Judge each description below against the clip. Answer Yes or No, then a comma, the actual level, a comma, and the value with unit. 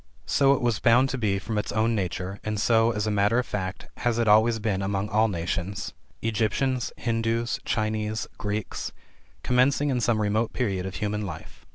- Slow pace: No, average, 185 wpm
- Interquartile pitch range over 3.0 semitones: No, narrow, 2.4 semitones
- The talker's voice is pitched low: Yes, low, 110 Hz